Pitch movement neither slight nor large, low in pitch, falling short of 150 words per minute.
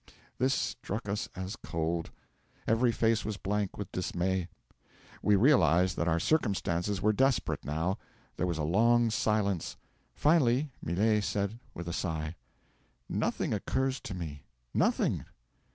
Yes: average, 4.7 semitones; low, 100 Hz; slow, 135 wpm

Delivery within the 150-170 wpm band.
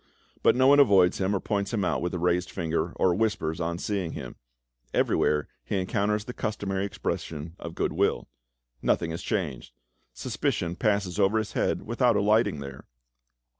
Yes: average, 165 wpm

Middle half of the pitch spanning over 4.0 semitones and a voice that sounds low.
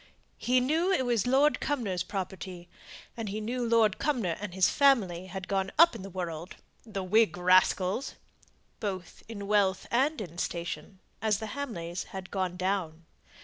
No: average, 4.4 semitones; high, 195 Hz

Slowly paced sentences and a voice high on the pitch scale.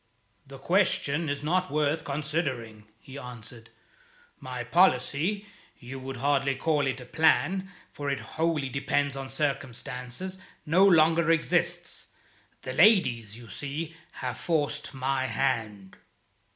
No: slow, 125 wpm; medium, 140 Hz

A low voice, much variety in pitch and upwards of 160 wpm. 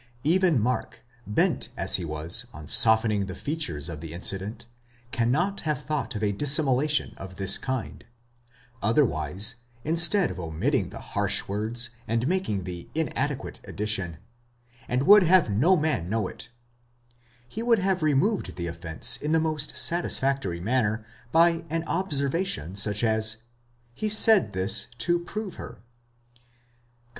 No: low, 120 Hz; wide, 8.5 semitones; average, 145 wpm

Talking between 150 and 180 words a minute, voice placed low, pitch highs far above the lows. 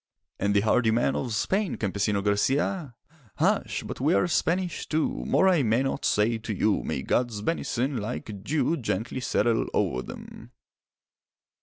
Yes: average, 155 wpm; low, 115 Hz; wide, 5.8 semitones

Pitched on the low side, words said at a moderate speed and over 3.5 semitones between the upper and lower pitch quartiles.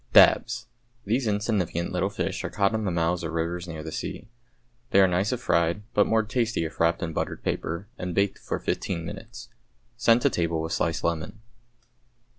Yes: very low, 90 Hz; average, 190 wpm; average, 4.1 semitones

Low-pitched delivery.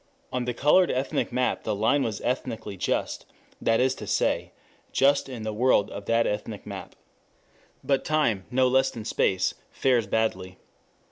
Yes: low, 120 Hz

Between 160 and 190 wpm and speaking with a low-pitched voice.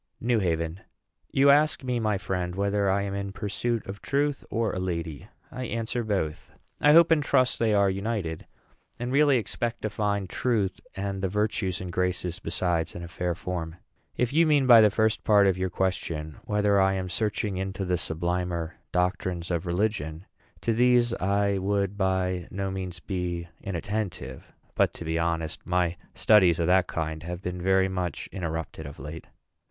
Yes: average, 180 wpm; very low, 95 Hz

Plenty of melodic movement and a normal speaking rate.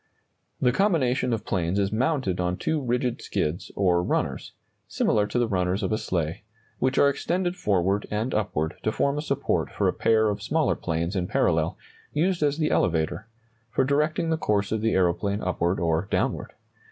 Yes: wide, 7.1 semitones; average, 185 wpm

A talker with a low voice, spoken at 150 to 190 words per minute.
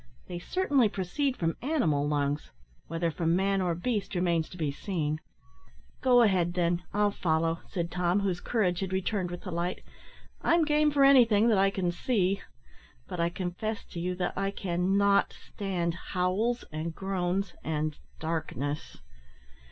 No: medium, 180 Hz; average, 160 wpm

